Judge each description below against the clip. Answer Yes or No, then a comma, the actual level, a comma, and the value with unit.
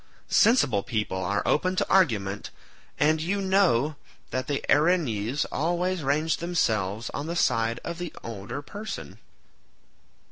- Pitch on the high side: No, medium, 145 Hz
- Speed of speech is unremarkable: No, slow, 130 wpm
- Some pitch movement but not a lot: No, wide, 7.6 semitones